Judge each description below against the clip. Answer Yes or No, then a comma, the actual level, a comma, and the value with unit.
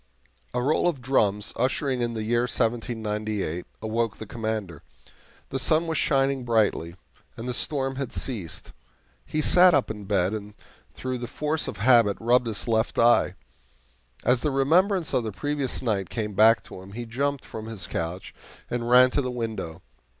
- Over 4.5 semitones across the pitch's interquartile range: No, average, 3.7 semitones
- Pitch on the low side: Yes, low, 120 Hz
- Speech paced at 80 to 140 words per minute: No, average, 170 wpm